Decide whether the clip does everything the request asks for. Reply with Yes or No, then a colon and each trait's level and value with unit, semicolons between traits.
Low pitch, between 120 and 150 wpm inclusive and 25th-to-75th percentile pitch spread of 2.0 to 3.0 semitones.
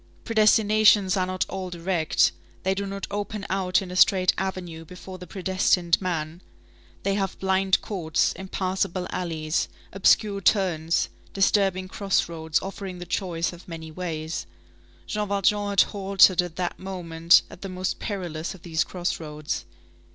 No: medium, 185 Hz; average, 145 wpm; narrow, 2.4 semitones